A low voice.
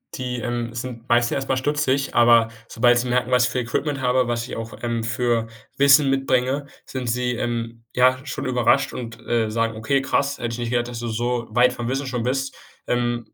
Yes: low, 125 Hz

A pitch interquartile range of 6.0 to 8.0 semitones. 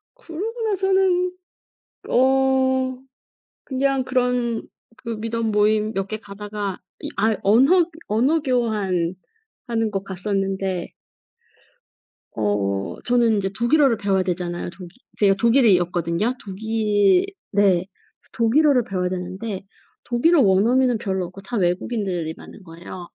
No: average, 5.2 semitones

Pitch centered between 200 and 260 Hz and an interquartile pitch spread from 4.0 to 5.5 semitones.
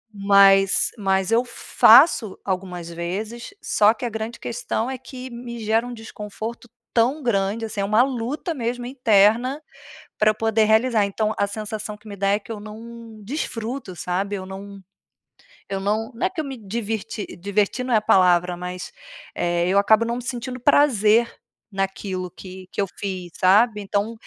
No: high, 215 Hz; average, 3.2 semitones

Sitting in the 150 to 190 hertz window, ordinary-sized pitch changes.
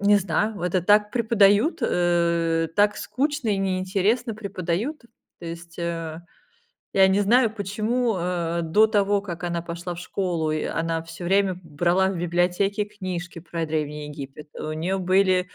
Yes: medium, 185 Hz; average, 3.3 semitones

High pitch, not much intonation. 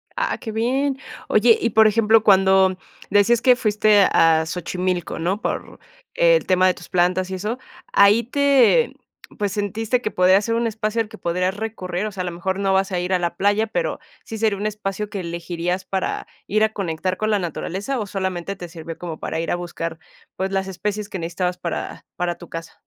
No: high, 195 Hz; average, 3.3 semitones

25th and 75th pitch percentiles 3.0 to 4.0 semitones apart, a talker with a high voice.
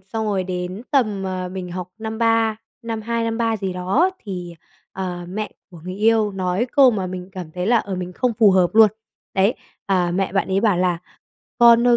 Yes: average, 3.7 semitones; high, 195 Hz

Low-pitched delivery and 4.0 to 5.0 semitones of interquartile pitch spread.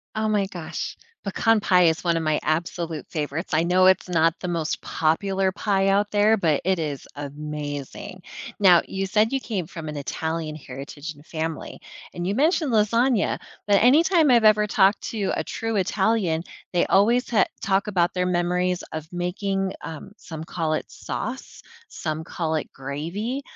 No: medium, 180 Hz; average, 4.5 semitones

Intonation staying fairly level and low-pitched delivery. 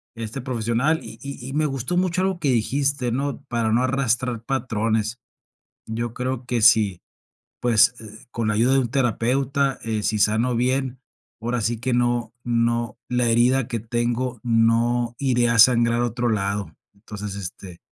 Yes: narrow, 2.3 semitones; low, 120 Hz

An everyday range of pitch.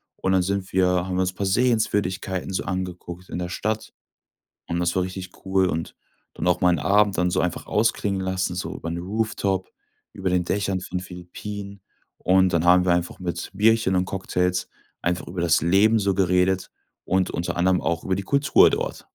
No: narrow, 1.6 semitones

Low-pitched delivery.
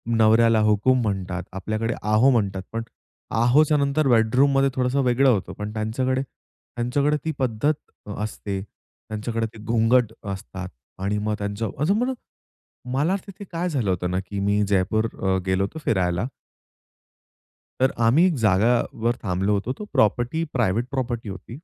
Yes: low, 115 Hz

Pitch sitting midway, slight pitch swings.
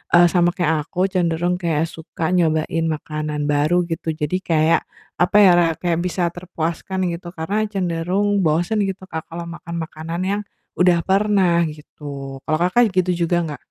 Yes: medium, 170 Hz; narrow, 2.3 semitones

